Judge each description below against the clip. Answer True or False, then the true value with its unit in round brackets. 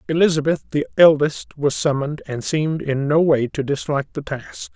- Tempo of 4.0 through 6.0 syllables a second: True (5.4 syllables/s)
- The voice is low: False (150 Hz)